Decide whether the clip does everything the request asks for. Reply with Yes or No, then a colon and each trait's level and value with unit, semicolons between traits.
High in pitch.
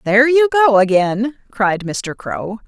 Yes: high, 235 Hz